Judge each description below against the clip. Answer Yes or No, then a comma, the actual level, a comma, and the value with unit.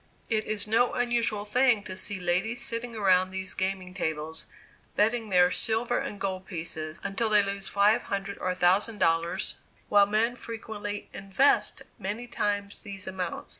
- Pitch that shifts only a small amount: No, average, 3.0 semitones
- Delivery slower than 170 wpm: Yes, average, 160 wpm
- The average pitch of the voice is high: Yes, high, 200 Hz